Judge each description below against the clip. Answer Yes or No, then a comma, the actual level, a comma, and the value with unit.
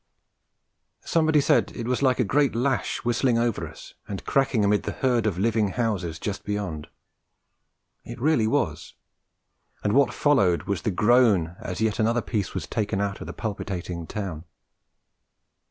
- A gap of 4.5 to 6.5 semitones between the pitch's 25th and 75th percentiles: No, average, 4.1 semitones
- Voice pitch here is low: Yes, low, 110 Hz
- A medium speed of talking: Yes, average, 155 wpm